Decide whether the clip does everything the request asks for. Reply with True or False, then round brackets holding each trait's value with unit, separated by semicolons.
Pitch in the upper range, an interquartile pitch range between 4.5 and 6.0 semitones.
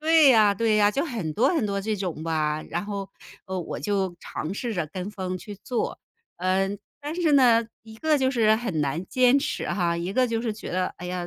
True (205 Hz; 4.9 semitones)